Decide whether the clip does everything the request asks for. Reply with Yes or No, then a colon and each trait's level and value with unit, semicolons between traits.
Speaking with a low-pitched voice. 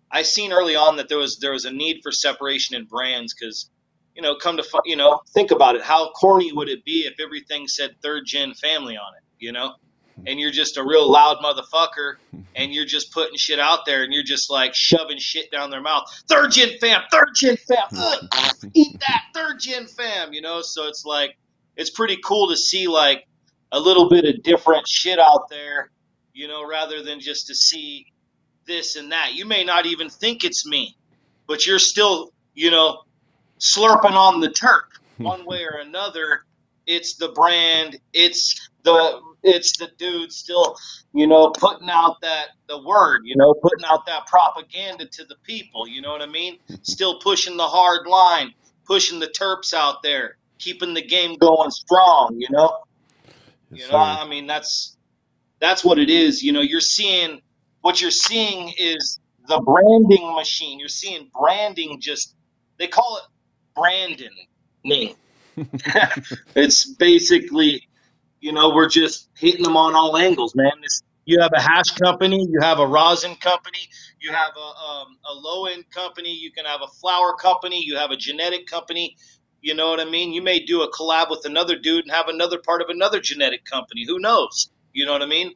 No: medium, 165 Hz